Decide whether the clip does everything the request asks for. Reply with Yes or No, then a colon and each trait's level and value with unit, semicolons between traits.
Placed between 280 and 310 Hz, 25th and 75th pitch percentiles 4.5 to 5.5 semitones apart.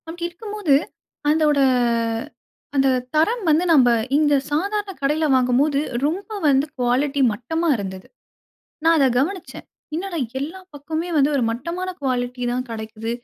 Yes: very high, 295 Hz; average, 5.0 semitones